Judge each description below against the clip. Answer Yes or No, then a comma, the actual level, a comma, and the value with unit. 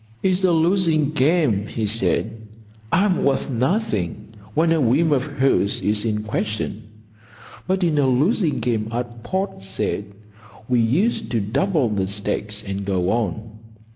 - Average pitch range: No, wide, 7.4 semitones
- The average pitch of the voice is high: No, low, 120 Hz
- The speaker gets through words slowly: No, average, 145 wpm